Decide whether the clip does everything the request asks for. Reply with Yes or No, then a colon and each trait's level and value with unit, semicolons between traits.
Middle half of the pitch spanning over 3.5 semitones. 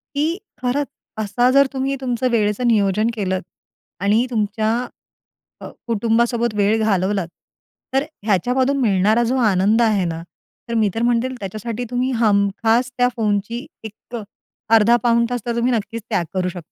No: average, 3.1 semitones